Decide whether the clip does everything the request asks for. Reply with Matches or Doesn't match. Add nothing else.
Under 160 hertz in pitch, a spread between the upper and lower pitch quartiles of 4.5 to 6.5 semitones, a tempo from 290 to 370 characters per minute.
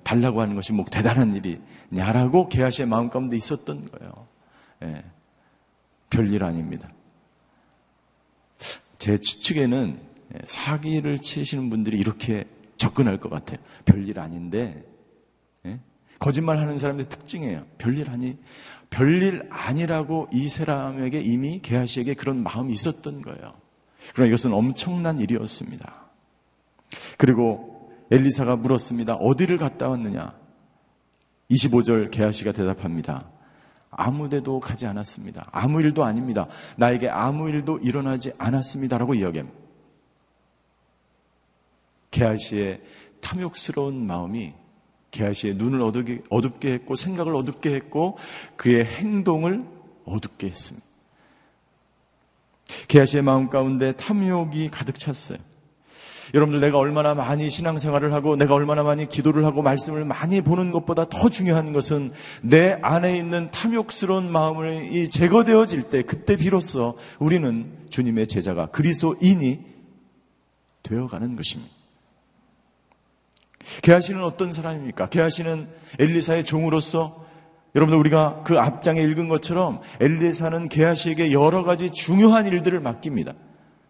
Matches